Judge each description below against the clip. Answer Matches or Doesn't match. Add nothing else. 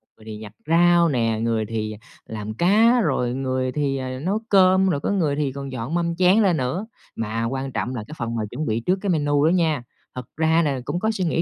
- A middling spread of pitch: Doesn't match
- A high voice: Doesn't match